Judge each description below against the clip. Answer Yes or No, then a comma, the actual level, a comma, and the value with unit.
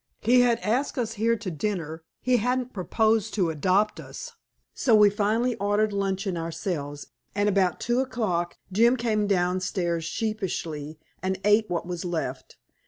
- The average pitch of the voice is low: No, high, 205 Hz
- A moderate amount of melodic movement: Yes, average, 4.2 semitones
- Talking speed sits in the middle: Yes, average, 150 wpm